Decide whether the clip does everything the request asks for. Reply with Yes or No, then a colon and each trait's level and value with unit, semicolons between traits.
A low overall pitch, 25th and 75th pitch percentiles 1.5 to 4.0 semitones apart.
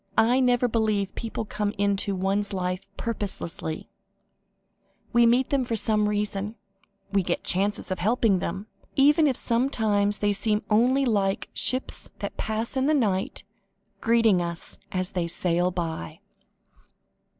No: high, 210 Hz; average, 3.4 semitones